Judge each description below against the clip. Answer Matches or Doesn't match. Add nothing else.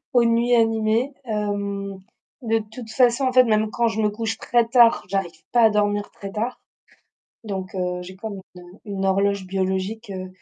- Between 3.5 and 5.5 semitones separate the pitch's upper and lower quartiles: Doesn't match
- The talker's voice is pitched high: Matches